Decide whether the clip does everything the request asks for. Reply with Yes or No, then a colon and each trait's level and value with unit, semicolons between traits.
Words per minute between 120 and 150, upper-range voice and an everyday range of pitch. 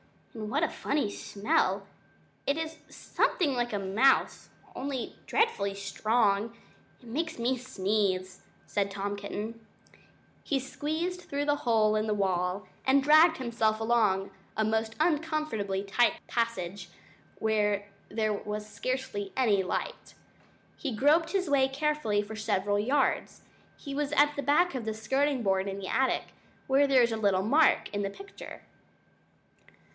No: average, 145 wpm; high, 225 Hz; wide, 5.7 semitones